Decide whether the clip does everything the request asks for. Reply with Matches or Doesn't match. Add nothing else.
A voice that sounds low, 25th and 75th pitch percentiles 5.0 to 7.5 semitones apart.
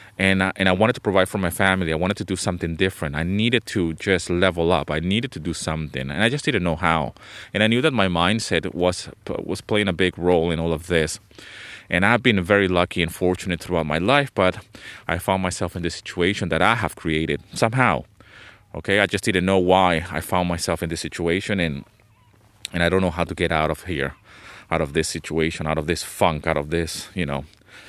Doesn't match